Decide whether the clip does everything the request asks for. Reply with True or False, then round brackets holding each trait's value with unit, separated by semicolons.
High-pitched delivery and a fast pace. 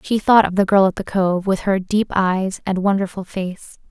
True (195 Hz; 230 wpm)